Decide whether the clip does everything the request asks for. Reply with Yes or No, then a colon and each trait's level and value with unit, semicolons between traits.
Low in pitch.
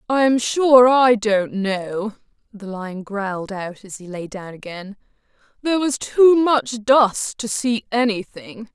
No: high, 220 Hz